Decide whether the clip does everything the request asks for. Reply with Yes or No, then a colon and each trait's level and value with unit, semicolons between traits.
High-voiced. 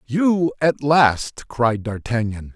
No: low, 130 Hz